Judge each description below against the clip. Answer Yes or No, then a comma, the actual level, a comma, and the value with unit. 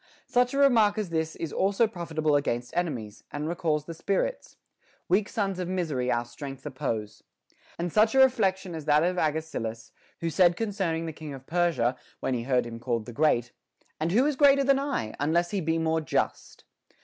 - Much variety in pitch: Yes, wide, 6.1 semitones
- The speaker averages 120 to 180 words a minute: No, average, 190 wpm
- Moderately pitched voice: Yes, medium, 165 Hz